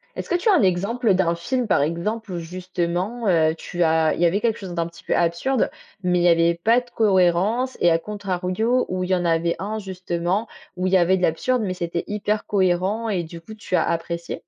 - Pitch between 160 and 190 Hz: Yes, medium, 185 Hz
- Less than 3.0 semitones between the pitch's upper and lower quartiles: No, average, 3.8 semitones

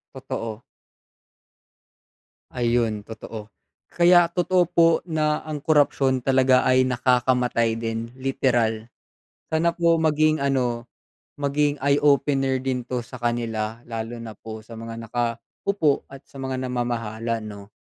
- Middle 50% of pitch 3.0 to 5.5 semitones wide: Yes, average, 3.9 semitones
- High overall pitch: No, low, 125 Hz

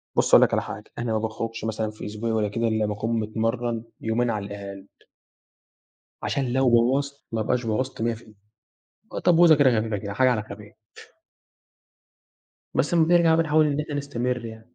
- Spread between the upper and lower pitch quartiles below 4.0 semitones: Yes, average, 3.5 semitones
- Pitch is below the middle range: Yes, low, 115 Hz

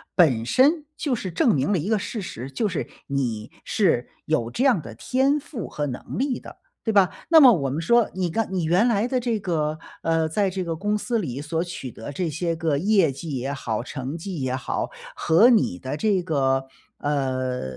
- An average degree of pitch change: No, wide, 7.5 semitones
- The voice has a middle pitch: Yes, medium, 165 Hz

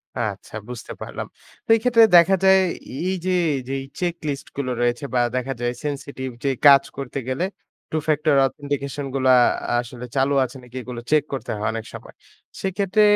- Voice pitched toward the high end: No, medium, 140 Hz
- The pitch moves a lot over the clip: No, average, 3.8 semitones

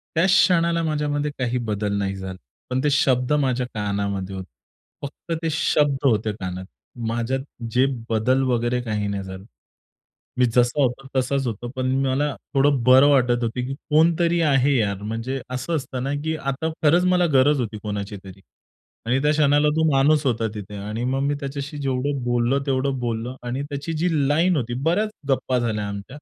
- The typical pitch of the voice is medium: No, low, 130 Hz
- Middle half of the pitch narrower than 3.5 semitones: No, average, 4.3 semitones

